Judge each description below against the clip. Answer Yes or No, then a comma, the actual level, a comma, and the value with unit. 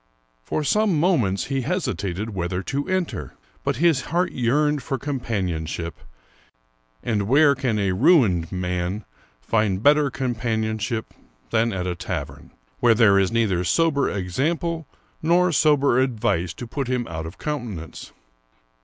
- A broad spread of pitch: Yes, wide, 7.3 semitones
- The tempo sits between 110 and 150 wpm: Yes, average, 145 wpm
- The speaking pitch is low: Yes, low, 115 Hz